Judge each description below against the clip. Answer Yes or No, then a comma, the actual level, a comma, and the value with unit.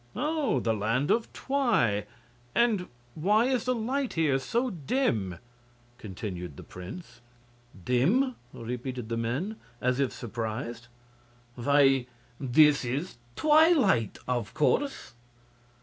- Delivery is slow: Yes, slow, 110 wpm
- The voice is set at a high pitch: No, low, 135 Hz